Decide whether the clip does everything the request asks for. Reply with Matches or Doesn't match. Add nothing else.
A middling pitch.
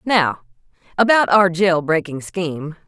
Matches